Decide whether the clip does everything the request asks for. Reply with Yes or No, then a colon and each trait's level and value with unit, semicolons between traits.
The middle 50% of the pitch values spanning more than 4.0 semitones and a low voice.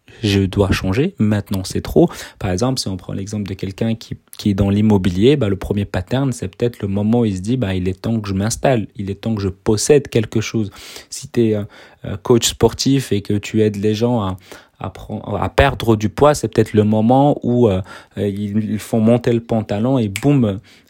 No: average, 3.1 semitones; low, 110 Hz